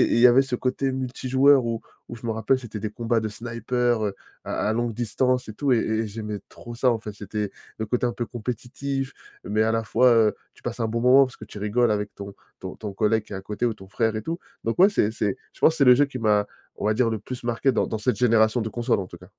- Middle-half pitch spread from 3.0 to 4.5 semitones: No, narrow, 2.6 semitones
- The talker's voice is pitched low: Yes, low, 115 Hz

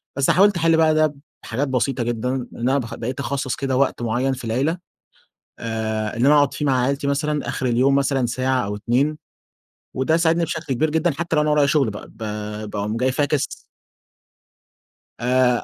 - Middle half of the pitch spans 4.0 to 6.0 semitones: No, average, 3.5 semitones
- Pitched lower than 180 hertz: Yes, low, 135 Hz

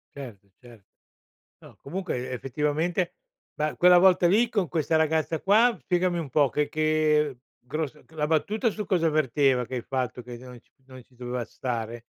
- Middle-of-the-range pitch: Yes, medium, 150 Hz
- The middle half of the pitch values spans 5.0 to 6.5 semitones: Yes, wide, 5.4 semitones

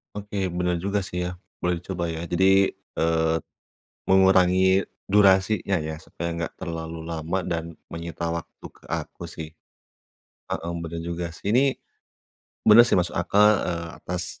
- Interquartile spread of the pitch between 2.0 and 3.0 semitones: Yes, narrow, 2.4 semitones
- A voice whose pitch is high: No, very low, 90 Hz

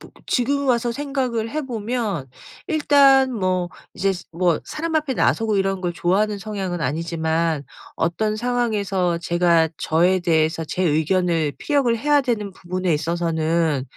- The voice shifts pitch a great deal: Yes, wide, 6.2 semitones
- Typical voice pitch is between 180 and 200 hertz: Yes, high, 190 Hz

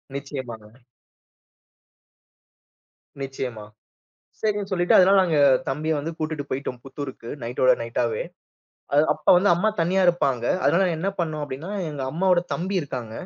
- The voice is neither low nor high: Yes, medium, 150 Hz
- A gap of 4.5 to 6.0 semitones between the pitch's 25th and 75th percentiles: Yes, average, 5.2 semitones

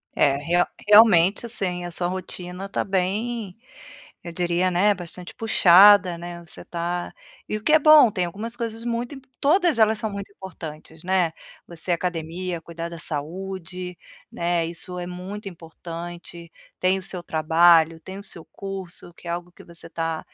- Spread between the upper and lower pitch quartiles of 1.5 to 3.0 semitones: Yes, average, 2.7 semitones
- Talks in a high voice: No, medium, 180 Hz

